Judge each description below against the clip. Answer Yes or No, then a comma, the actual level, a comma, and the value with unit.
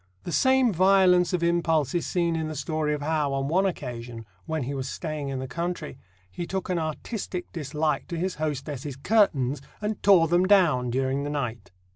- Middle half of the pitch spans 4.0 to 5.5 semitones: Yes, average, 4.4 semitones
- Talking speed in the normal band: Yes, average, 190 wpm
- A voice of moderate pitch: Yes, medium, 155 Hz